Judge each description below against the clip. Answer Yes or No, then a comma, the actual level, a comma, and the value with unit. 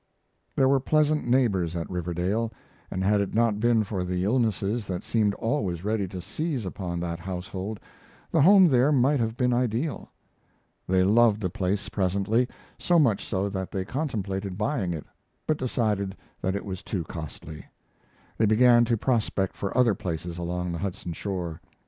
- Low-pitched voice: Yes, low, 100 Hz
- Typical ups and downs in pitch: Yes, average, 4.6 semitones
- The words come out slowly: No, average, 165 wpm